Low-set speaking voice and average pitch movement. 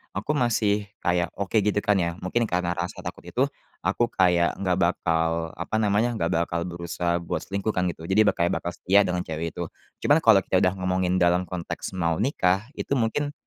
Yes: very low, 90 Hz; average, 3.1 semitones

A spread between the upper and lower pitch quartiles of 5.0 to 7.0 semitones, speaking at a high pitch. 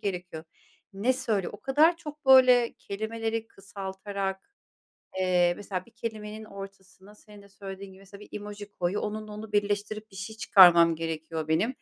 No: narrow, 2.4 semitones; high, 205 Hz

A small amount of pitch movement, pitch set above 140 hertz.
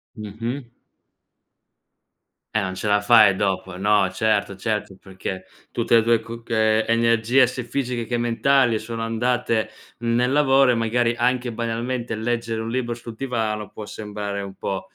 No: narrow, 2.1 semitones; low, 115 Hz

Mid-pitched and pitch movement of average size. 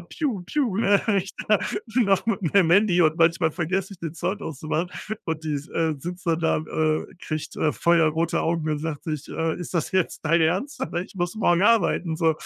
Yes: medium, 170 Hz; average, 3.2 semitones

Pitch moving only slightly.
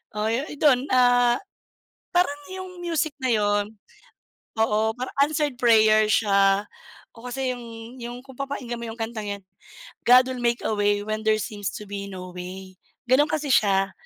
No: average, 3.7 semitones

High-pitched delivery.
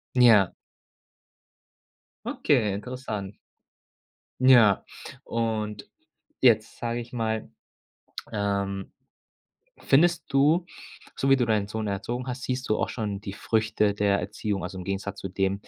No: low, 110 Hz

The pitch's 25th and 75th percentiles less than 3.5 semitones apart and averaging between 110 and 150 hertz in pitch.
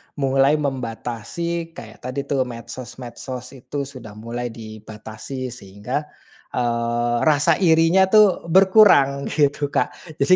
No: average, 4.3 semitones; low, 135 Hz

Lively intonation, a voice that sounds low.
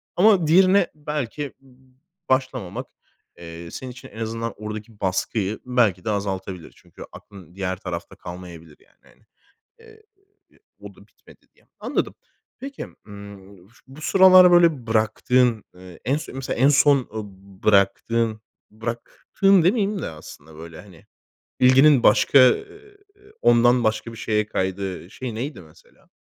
Yes: wide, 6.8 semitones; low, 115 Hz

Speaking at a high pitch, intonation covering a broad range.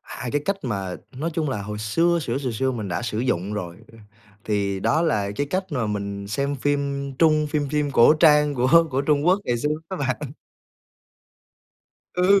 No: low, 135 Hz; wide, 6.1 semitones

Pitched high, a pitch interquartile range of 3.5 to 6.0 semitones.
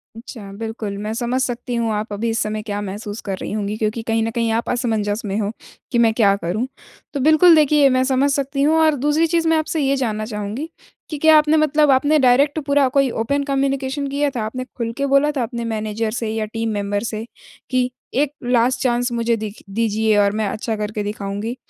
Yes: high, 235 Hz; average, 4.4 semitones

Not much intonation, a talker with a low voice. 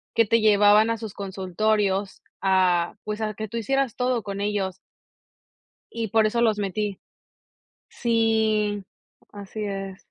No: narrow, 2.1 semitones; high, 210 Hz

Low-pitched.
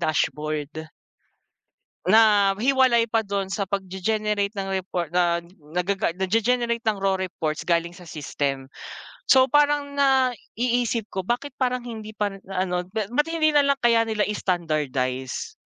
No: high, 200 Hz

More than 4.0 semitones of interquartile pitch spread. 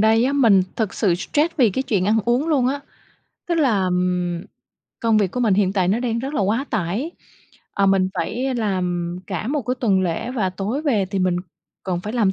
Yes: average, 5.1 semitones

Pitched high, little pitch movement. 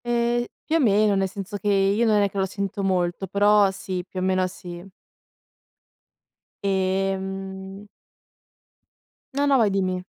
Yes: high, 195 Hz; narrow, 1.5 semitones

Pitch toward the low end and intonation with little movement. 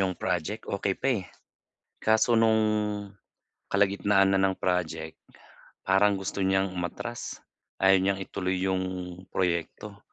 Yes: very low, 95 Hz; narrow, 1.7 semitones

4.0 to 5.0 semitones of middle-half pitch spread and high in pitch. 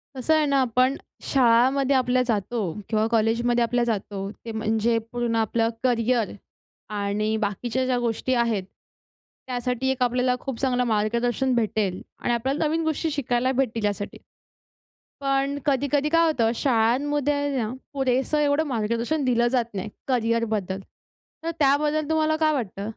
No: average, 3.4 semitones; high, 245 Hz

